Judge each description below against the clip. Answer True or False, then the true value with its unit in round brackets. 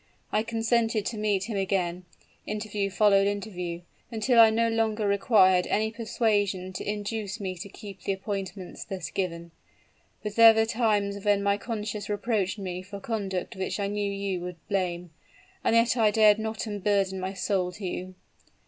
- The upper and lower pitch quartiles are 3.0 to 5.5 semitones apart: False (2.5 semitones)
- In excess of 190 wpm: False (165 wpm)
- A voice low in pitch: False (205 Hz)